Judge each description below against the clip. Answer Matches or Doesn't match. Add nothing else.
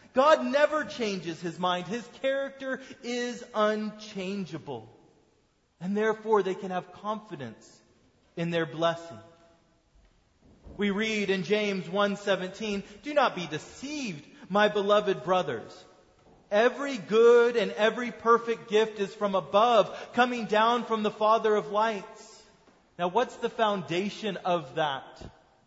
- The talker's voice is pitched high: Matches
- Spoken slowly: Matches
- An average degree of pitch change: Matches